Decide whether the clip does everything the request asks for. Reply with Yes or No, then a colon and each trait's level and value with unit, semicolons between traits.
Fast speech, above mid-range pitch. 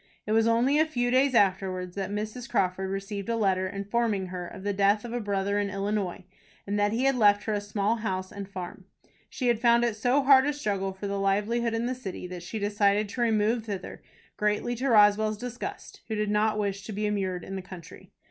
Yes: fast, 225 wpm; high, 210 Hz